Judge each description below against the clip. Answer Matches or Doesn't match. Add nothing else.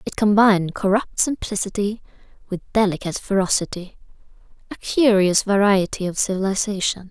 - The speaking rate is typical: Doesn't match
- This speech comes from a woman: Matches